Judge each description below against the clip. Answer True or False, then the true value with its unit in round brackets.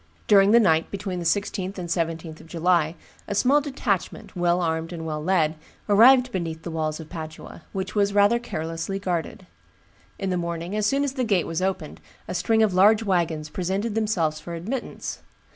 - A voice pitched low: False (180 Hz)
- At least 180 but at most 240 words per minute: True (185 wpm)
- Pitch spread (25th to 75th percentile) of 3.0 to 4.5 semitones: True (3.9 semitones)